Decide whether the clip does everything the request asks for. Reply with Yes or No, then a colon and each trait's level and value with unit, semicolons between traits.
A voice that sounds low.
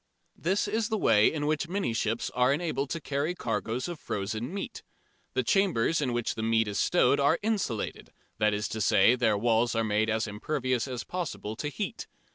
Yes: low, 125 Hz